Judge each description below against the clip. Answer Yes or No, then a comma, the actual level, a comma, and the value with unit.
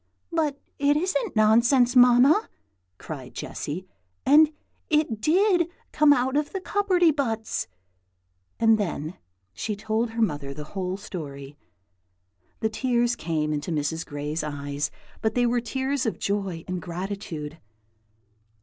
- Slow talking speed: Yes, slow, 130 wpm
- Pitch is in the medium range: No, high, 220 Hz